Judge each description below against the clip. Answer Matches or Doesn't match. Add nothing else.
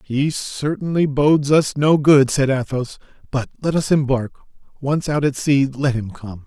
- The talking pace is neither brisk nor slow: Matches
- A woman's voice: Doesn't match